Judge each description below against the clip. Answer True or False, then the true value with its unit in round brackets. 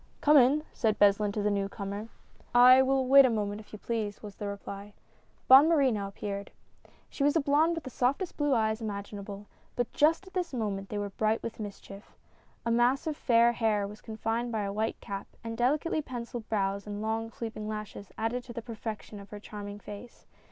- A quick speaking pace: True (215 wpm)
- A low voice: False (220 Hz)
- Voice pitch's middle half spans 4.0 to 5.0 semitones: False (3.6 semitones)